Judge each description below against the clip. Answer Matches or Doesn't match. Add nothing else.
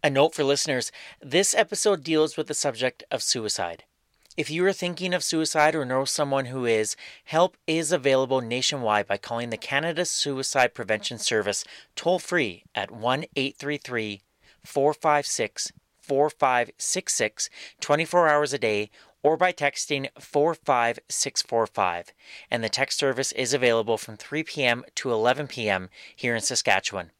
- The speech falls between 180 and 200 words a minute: Doesn't match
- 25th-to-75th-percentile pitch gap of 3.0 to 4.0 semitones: Doesn't match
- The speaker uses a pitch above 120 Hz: Matches